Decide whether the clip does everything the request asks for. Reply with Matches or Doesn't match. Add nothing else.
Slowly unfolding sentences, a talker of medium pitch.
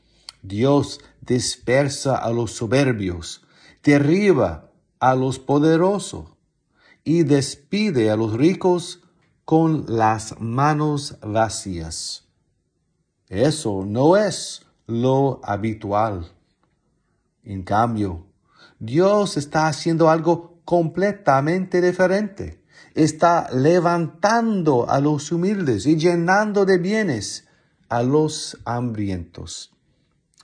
Matches